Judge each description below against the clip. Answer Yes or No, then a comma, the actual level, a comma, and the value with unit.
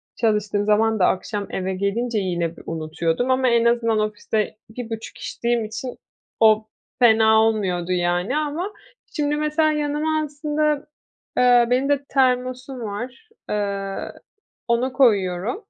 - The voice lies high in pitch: Yes, high, 230 Hz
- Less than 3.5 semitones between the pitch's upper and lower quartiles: No, average, 4.4 semitones